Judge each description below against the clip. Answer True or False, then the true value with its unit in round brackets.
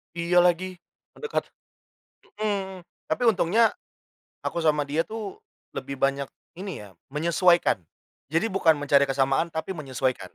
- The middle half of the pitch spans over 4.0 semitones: True (4.7 semitones)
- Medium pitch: True (170 Hz)